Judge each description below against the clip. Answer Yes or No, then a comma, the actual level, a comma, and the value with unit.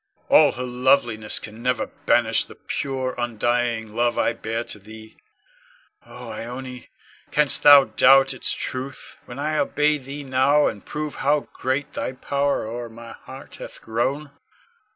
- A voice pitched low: Yes, low, 125 Hz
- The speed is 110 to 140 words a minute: No, average, 150 wpm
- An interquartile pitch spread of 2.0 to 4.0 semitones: Yes, average, 3.1 semitones